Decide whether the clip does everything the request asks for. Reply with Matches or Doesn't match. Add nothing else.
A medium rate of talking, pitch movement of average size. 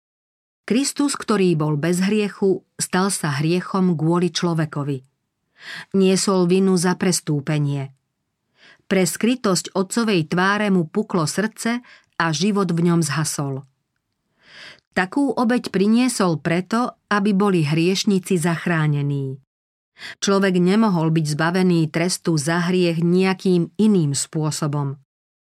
Doesn't match